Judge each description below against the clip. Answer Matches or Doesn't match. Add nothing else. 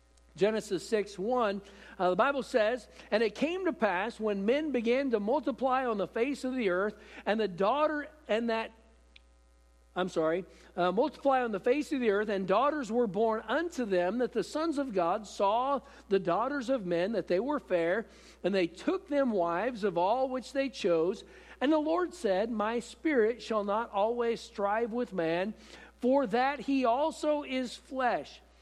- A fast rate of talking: Doesn't match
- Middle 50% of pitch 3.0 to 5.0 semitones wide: Doesn't match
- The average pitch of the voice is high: Matches